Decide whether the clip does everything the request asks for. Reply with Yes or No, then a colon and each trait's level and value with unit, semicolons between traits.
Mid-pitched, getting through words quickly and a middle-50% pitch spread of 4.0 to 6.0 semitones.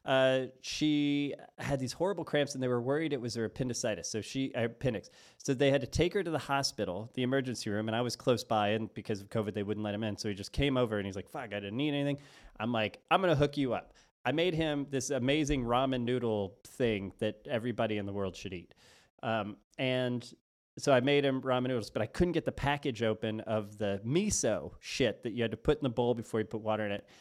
No: low, 125 Hz; fast, 245 wpm; average, 4.4 semitones